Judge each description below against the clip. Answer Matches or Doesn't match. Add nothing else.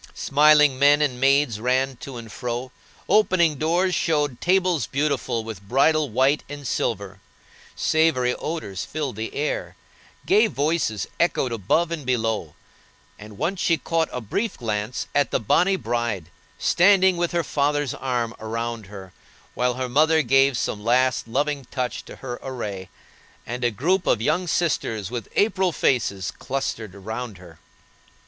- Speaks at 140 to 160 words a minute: Matches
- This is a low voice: Matches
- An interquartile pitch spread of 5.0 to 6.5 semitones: Matches